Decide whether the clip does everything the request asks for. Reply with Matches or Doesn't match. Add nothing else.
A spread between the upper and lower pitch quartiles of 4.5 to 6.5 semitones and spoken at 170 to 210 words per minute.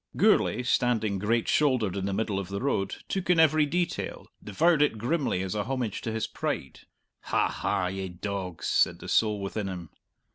Matches